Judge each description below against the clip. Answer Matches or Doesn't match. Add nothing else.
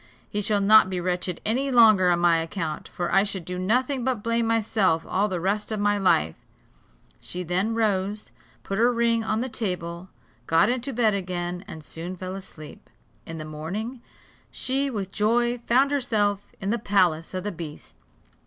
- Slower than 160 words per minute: Doesn't match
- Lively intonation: Doesn't match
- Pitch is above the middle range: Matches